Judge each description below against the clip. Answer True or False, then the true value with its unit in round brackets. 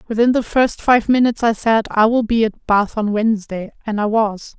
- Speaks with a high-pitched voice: True (220 Hz)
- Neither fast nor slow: False (225 wpm)